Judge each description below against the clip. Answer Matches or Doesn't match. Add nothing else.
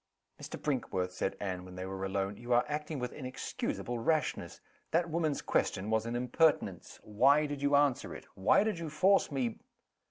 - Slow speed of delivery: Doesn't match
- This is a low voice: Matches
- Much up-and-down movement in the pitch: Matches